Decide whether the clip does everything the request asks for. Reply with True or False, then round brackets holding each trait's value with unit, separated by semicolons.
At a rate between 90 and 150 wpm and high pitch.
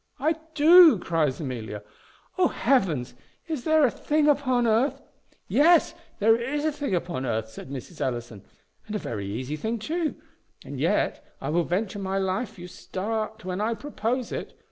False (170 wpm; 215 Hz)